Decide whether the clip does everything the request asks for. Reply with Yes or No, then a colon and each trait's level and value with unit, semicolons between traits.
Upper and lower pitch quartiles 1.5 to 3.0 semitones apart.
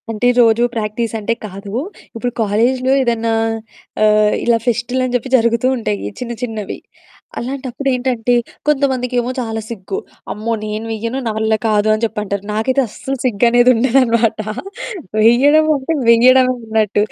Yes: average, 2.7 semitones